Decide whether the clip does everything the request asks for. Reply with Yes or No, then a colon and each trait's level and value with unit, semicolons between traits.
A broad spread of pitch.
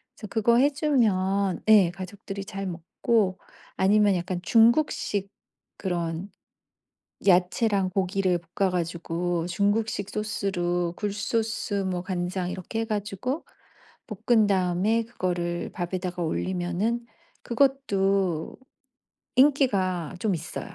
No: average, 3.5 semitones